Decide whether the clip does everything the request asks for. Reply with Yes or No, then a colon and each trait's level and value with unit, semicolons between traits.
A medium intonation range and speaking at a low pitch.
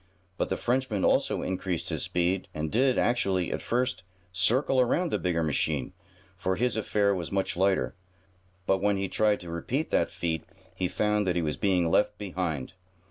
Yes: average, 3.5 semitones; very low, 95 Hz